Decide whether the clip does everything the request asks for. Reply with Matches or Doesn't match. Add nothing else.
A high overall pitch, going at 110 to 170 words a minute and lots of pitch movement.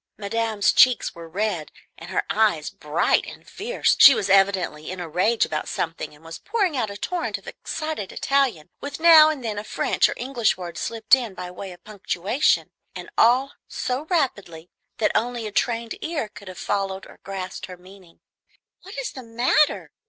Doesn't match